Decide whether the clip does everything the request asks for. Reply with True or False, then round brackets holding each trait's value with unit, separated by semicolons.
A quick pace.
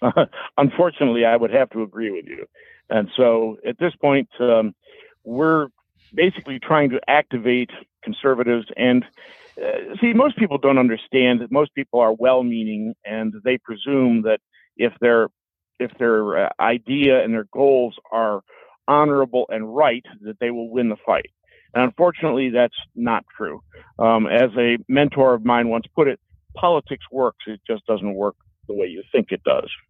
False (165 wpm)